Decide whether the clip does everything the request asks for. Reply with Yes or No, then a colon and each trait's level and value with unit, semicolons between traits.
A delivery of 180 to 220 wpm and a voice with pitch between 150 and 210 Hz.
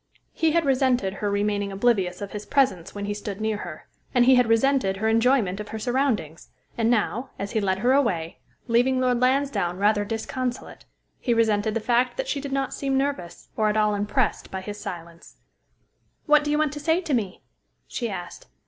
No: average, 200 wpm; high, 225 Hz